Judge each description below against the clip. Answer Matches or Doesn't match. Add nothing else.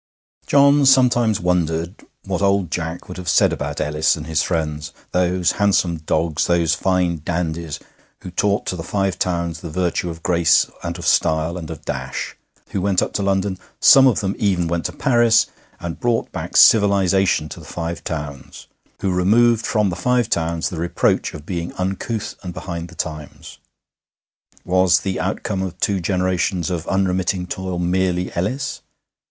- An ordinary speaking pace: Matches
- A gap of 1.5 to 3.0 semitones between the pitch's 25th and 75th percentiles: Matches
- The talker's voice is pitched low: Matches